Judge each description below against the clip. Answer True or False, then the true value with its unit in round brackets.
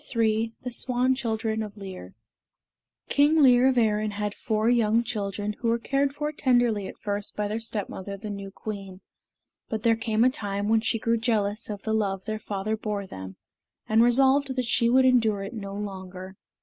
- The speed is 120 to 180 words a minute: False (190 wpm)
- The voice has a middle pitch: False (220 Hz)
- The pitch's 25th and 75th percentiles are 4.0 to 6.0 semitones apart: False (2.9 semitones)